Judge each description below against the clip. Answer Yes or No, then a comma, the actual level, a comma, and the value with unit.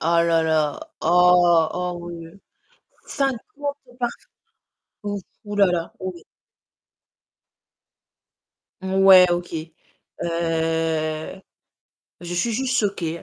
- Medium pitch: Yes, medium, 175 Hz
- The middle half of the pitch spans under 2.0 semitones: No, narrow, 2.6 semitones